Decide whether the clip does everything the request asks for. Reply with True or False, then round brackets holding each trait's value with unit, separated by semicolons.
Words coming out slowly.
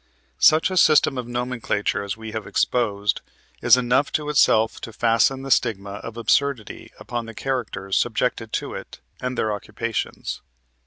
False (155 wpm)